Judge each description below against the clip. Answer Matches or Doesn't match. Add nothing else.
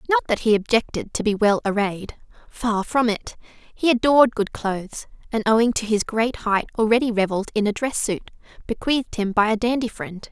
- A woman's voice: Matches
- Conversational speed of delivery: Matches